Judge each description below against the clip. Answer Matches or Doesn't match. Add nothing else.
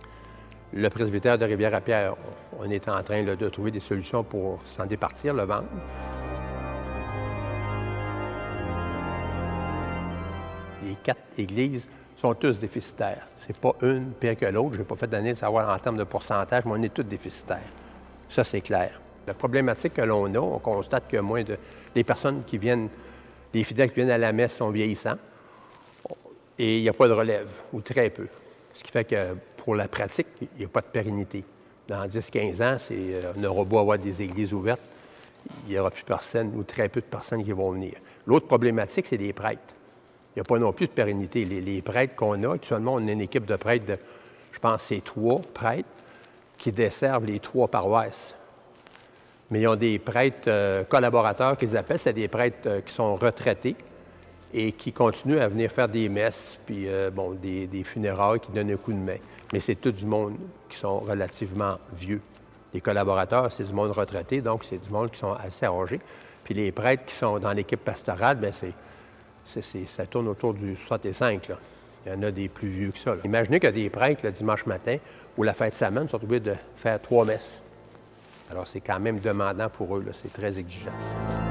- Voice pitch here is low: Matches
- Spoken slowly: Doesn't match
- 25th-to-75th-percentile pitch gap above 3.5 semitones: Doesn't match